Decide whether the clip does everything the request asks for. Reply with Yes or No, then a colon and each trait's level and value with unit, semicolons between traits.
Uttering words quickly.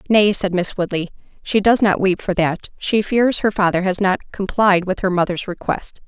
No: average, 195 wpm